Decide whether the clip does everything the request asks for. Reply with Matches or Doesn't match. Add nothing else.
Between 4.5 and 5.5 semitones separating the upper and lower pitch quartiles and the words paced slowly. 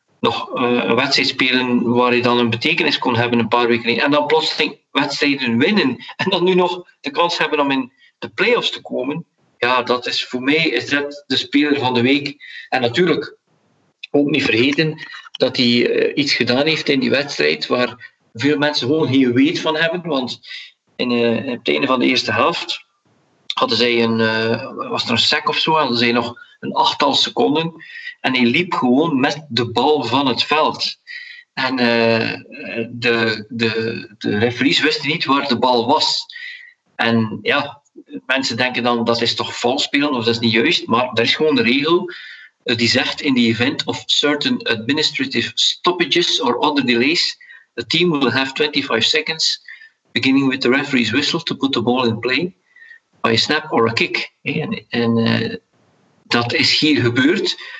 Doesn't match